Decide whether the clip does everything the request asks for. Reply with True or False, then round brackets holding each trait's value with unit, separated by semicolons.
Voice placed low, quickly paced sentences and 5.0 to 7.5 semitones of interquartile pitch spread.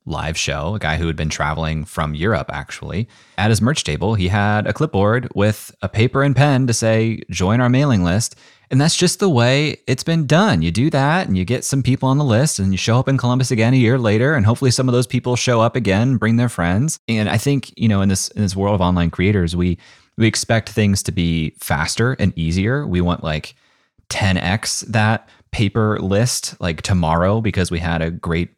True (110 Hz; 225 wpm; 5.6 semitones)